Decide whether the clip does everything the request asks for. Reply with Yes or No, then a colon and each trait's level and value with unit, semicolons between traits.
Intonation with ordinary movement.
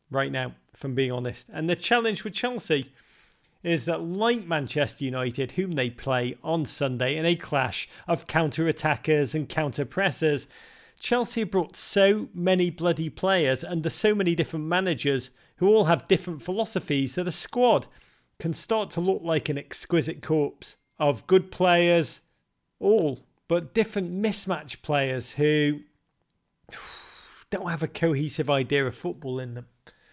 Yes: average, 4.2 semitones